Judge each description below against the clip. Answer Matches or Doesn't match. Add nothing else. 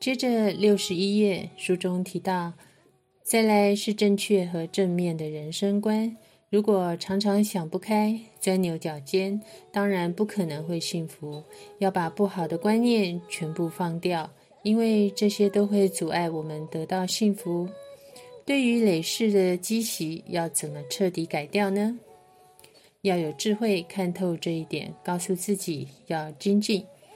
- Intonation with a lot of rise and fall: Doesn't match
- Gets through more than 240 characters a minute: Doesn't match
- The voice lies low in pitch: Doesn't match